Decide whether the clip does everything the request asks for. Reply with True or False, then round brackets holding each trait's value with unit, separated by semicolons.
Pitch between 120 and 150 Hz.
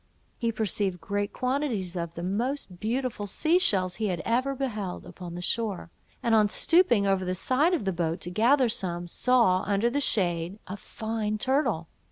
False (210 Hz)